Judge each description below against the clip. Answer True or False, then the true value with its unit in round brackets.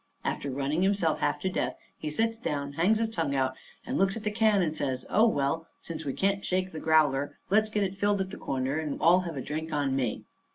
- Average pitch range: False (5.8 semitones)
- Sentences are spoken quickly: True (240 wpm)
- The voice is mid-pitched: True (165 Hz)